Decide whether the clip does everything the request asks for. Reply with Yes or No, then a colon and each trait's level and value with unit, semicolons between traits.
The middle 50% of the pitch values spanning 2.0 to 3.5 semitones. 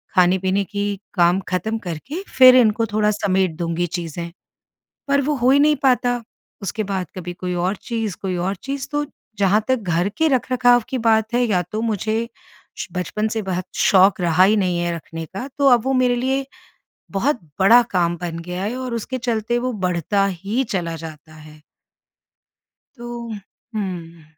No: average, 5.2 semitones